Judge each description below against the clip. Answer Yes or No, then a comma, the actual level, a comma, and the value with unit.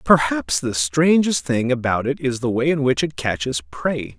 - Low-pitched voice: Yes, low, 130 Hz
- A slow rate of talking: No, average, 200 wpm